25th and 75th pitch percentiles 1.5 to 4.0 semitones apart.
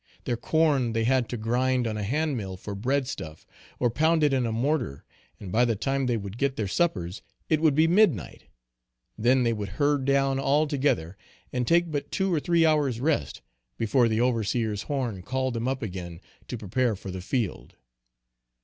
No: average, 4.7 semitones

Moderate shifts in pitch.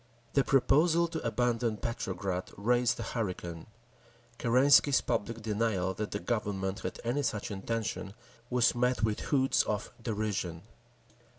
Yes: average, 3.6 semitones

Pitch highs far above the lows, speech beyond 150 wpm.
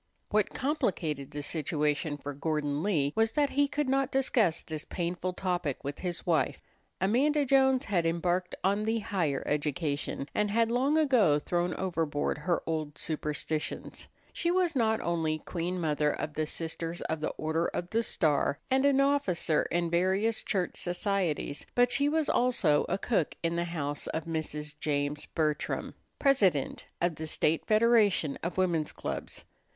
Yes: wide, 6.5 semitones; average, 160 wpm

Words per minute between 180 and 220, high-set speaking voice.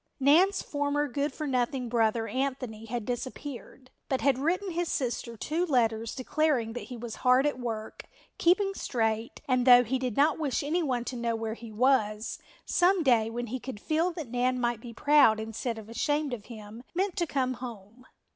Yes: average, 185 wpm; very high, 250 Hz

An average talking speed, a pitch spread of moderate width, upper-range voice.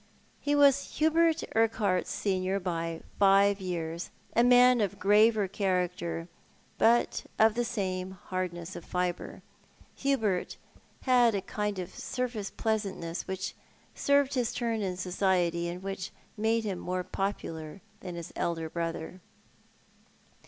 No: slow, 125 wpm; average, 4.0 semitones; high, 195 Hz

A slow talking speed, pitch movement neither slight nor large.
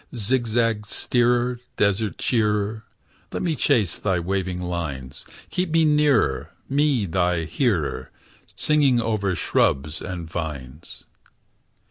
No: slow, 105 wpm; wide, 6.0 semitones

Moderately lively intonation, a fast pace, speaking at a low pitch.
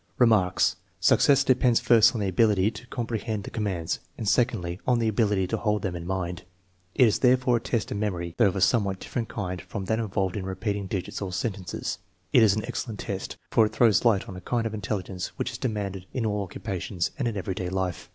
Yes: average, 3.3 semitones; fast, 225 wpm; low, 105 Hz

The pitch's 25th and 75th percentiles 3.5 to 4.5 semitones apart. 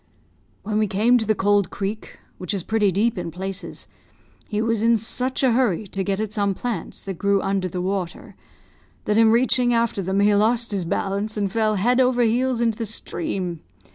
No: average, 2.9 semitones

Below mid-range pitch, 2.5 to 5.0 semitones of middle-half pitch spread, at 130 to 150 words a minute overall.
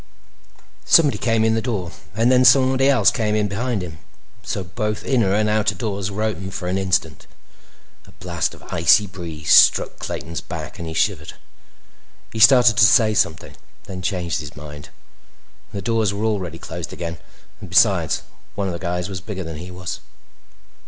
No: low, 100 Hz; average, 4.1 semitones; average, 180 wpm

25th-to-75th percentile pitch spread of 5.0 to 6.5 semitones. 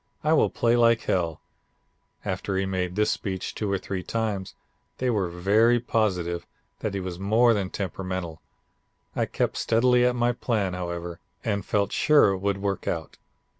No: average, 3.7 semitones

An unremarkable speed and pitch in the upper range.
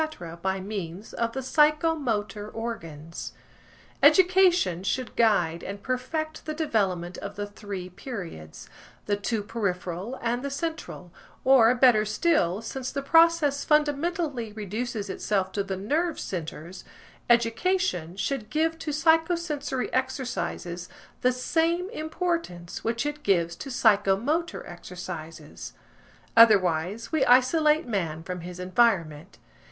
No: slow, 115 wpm; high, 230 Hz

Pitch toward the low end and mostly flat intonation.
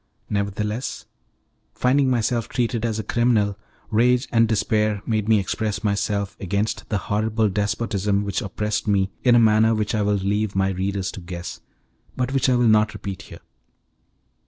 Yes: low, 105 Hz; narrow, 2.1 semitones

